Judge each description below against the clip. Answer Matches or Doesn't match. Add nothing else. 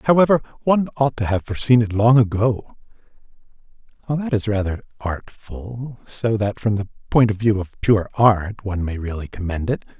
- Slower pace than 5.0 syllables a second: Doesn't match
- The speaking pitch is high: Doesn't match